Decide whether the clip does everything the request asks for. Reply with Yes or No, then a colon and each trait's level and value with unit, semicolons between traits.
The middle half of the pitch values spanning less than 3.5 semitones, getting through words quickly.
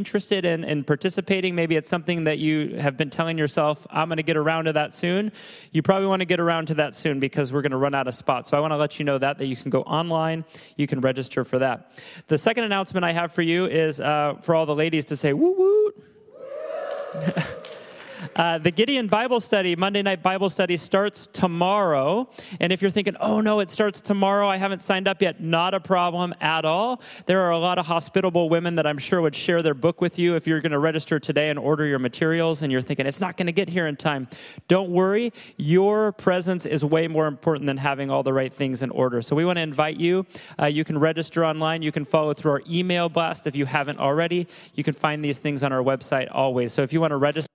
No: average, 3.8 semitones; fast, 245 wpm